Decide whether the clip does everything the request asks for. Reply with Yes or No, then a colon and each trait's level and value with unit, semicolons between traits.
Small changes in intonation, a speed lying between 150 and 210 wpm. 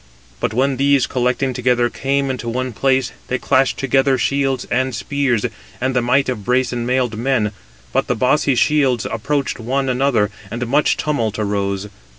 Yes: narrow, 2.2 semitones; average, 160 wpm